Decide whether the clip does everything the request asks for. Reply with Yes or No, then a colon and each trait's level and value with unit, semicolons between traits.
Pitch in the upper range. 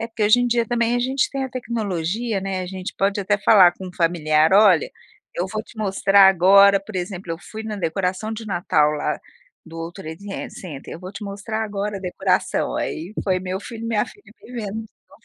Yes: high, 195 Hz